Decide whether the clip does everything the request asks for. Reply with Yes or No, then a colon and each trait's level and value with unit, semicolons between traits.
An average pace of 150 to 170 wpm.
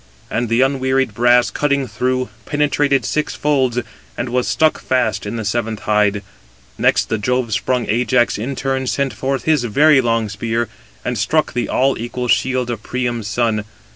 Yes: average, 165 wpm